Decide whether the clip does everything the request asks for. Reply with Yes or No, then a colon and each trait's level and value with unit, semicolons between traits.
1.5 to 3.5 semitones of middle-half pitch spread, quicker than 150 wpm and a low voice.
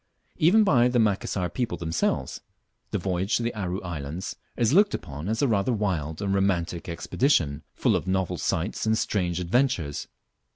No: average, 5.2 semitones; average, 165 wpm; very low, 95 Hz